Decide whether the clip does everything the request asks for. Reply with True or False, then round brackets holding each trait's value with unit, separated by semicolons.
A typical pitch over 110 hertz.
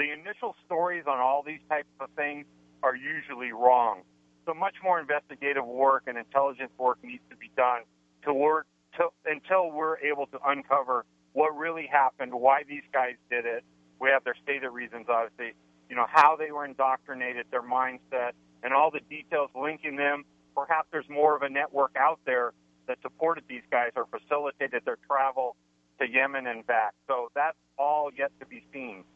True (140 Hz)